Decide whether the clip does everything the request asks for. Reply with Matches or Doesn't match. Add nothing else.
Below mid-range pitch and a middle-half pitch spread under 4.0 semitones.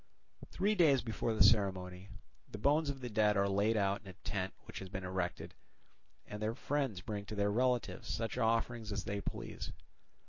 Matches